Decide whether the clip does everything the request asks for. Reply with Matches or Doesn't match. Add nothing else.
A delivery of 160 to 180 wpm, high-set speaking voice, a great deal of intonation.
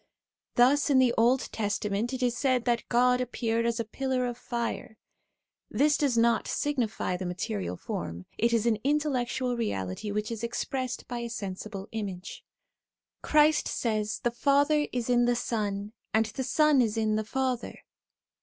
Doesn't match